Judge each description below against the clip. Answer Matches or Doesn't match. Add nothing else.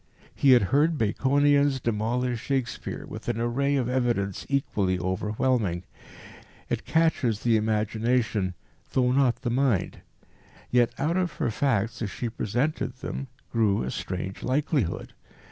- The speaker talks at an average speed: Doesn't match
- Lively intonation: Doesn't match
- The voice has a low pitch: Matches